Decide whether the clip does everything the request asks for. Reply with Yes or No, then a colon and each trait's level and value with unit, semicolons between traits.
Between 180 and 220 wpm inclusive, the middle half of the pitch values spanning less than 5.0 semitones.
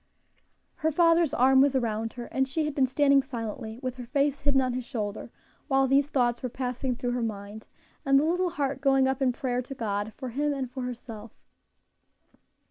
Yes: average, 200 wpm; narrow, 2.5 semitones